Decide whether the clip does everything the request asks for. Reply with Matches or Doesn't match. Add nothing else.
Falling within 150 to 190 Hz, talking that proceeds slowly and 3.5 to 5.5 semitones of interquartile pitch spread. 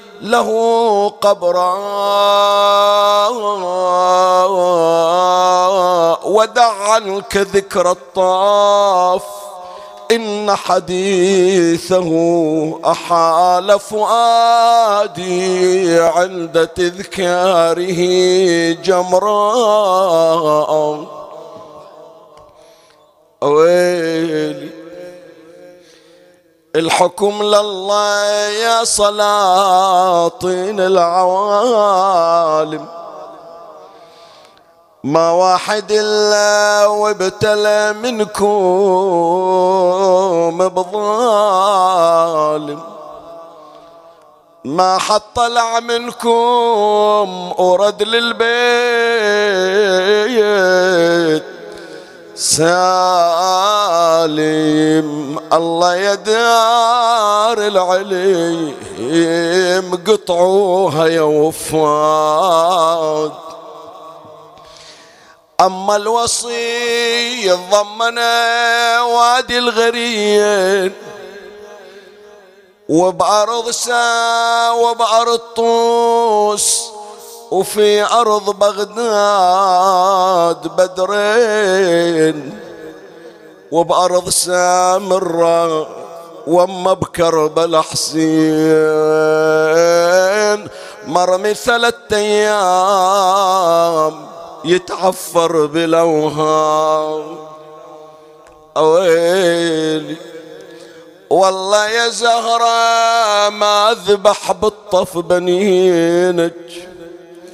Matches